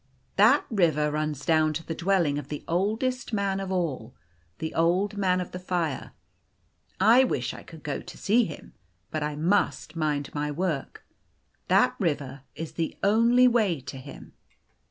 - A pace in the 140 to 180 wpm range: Yes, average, 170 wpm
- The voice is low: No, medium, 165 Hz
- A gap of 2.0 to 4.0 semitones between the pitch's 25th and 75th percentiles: No, average, 4.7 semitones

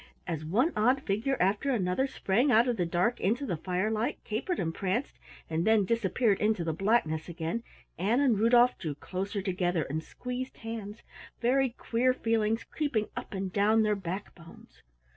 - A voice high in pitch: Yes, high, 215 Hz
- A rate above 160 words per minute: Yes, average, 170 wpm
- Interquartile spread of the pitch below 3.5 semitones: No, average, 4.7 semitones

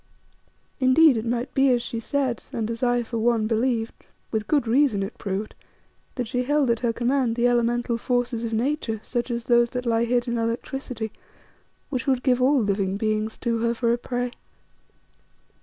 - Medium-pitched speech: No, high, 240 Hz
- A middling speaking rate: Yes, average, 185 wpm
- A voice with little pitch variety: Yes, narrow, 1.8 semitones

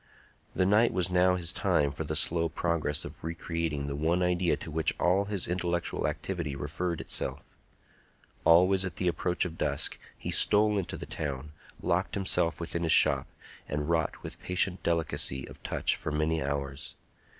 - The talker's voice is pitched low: Yes, very low, 85 Hz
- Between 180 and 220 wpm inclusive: No, average, 170 wpm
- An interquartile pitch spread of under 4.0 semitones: Yes, average, 2.9 semitones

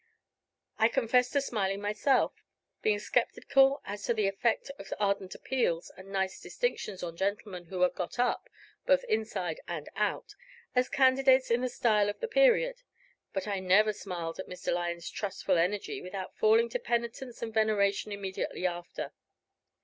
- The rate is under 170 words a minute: Yes, average, 155 wpm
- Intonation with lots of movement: No, average, 4.6 semitones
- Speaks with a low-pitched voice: No, high, 210 Hz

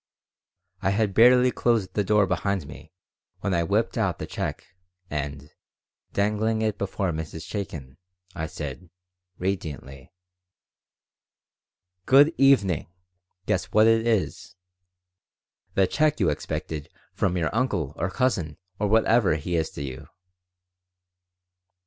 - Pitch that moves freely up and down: Yes, wide, 5.8 semitones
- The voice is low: Yes, very low, 95 Hz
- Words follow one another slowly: Yes, slow, 120 wpm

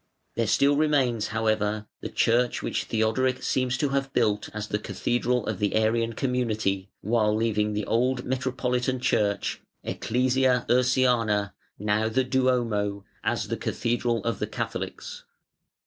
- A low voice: Yes, low, 115 Hz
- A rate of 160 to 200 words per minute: No, slow, 135 wpm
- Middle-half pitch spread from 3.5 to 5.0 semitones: No, average, 3.1 semitones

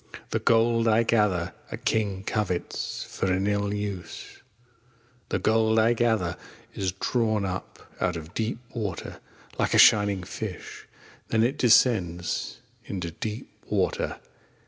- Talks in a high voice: No, low, 105 Hz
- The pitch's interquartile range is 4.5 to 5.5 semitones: No, average, 3.4 semitones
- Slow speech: Yes, slow, 130 wpm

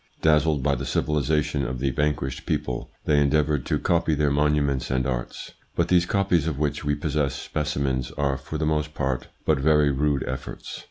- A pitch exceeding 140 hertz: No, very low, 75 Hz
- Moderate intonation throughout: No, narrow, 2.2 semitones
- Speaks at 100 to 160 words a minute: No, average, 180 wpm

